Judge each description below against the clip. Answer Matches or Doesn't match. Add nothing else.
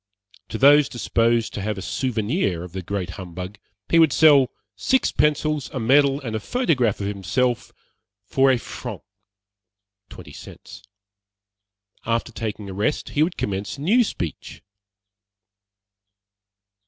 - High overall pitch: Doesn't match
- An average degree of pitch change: Doesn't match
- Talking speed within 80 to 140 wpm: Matches